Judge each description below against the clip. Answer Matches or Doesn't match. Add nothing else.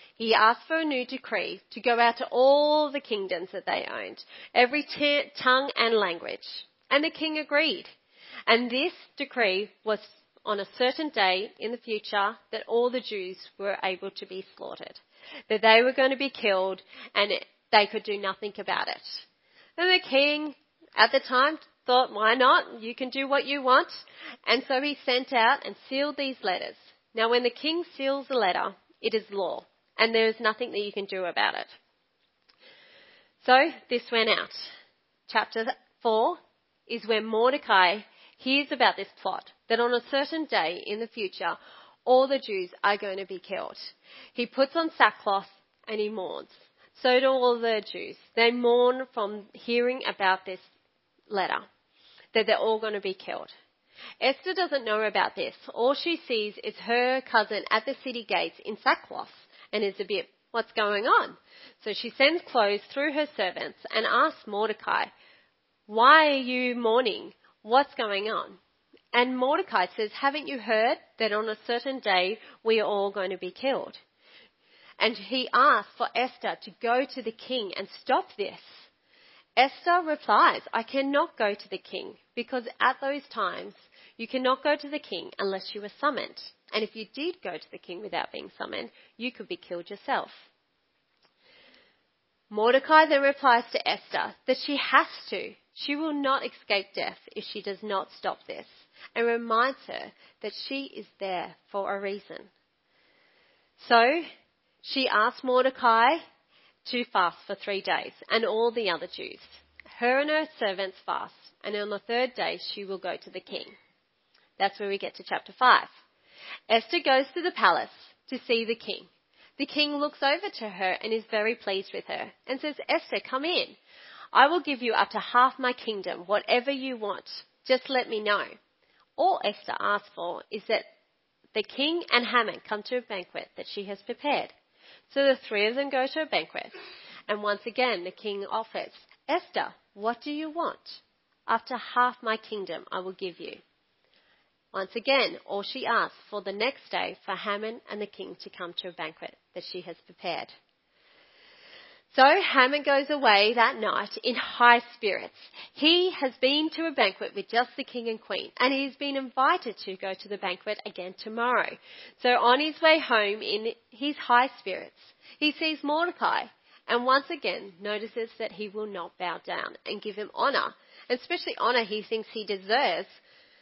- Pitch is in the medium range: Doesn't match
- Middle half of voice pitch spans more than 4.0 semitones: Matches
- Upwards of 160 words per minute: Matches